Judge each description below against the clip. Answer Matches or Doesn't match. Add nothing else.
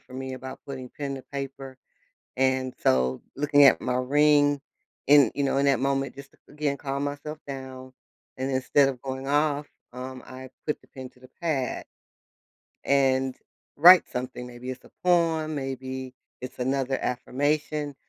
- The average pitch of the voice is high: Doesn't match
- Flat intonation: Matches